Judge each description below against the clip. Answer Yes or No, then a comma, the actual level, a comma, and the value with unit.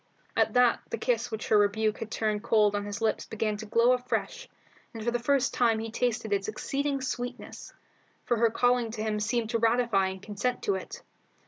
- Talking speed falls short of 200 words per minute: No, fast, 205 wpm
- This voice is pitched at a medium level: No, high, 225 Hz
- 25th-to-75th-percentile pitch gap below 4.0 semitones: Yes, narrow, 2.5 semitones